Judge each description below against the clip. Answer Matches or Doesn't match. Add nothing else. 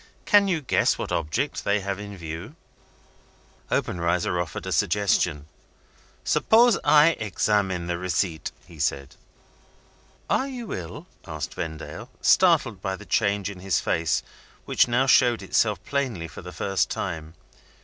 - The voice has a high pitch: Doesn't match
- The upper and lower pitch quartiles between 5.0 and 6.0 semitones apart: Matches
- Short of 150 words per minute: Matches